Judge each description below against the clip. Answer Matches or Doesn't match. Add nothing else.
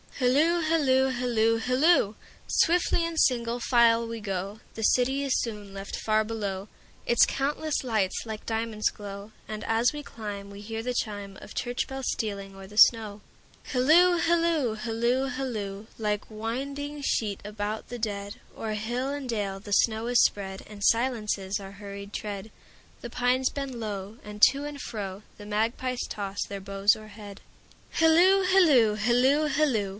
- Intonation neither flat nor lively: Matches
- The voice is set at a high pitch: Matches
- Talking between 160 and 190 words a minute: Doesn't match